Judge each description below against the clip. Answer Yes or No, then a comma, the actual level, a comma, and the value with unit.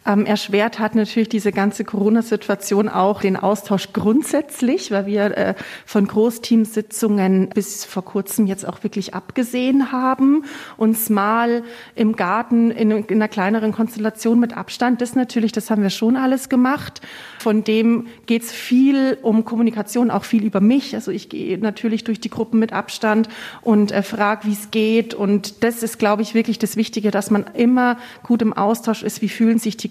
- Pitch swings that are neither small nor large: No, narrow, 2.0 semitones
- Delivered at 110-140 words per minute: No, average, 175 wpm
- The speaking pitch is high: Yes, high, 220 Hz